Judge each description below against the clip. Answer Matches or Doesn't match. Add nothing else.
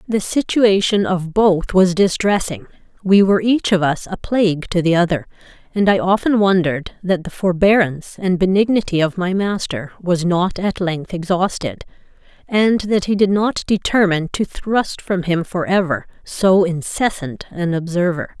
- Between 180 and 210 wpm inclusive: Doesn't match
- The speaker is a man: Doesn't match